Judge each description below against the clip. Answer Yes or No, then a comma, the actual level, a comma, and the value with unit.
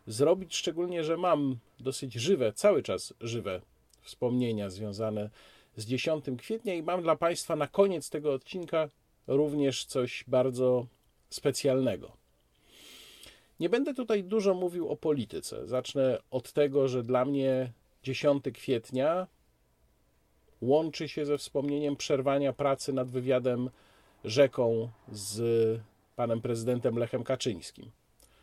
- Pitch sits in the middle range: No, low, 130 Hz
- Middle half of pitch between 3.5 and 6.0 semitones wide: Yes, average, 4.2 semitones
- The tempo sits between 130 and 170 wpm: No, average, 115 wpm